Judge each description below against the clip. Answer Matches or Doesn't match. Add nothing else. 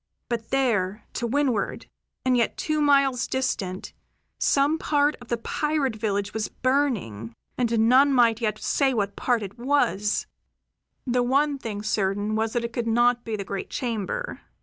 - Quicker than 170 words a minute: Doesn't match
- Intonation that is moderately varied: Matches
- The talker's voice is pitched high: Matches